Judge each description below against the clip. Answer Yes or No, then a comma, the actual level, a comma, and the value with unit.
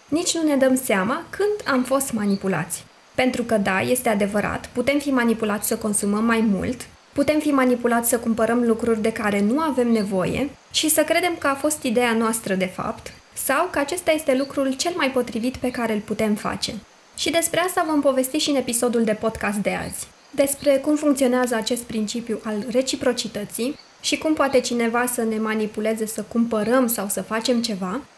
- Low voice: No, high, 245 Hz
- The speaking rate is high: Yes, fast, 185 wpm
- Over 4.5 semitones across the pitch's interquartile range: No, average, 4.2 semitones